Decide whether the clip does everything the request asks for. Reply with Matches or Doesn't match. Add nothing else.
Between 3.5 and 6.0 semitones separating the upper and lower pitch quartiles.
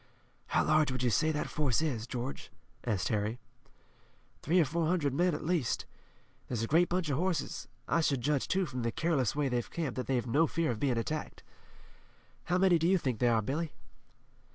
Matches